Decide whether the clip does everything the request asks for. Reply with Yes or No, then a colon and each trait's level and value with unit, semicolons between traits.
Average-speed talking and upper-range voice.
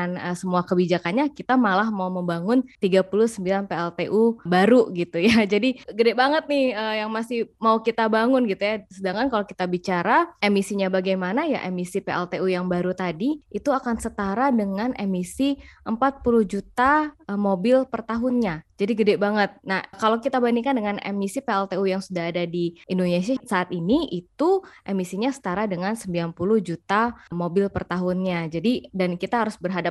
No: fast, 155 wpm; high, 200 Hz